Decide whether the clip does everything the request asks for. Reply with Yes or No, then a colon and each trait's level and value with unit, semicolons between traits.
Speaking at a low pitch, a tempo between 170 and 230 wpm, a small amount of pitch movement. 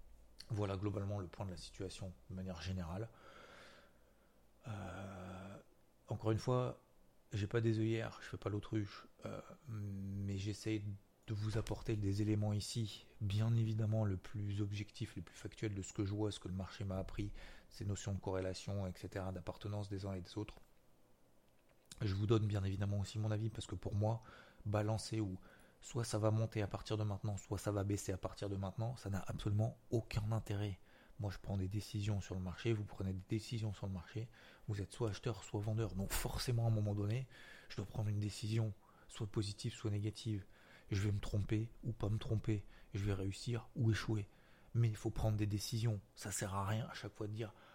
Yes: low, 105 Hz; average, 200 wpm; narrow, 2.0 semitones